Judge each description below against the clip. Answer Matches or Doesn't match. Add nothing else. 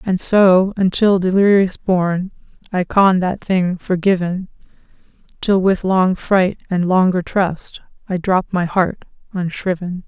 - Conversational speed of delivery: Doesn't match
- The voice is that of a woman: Matches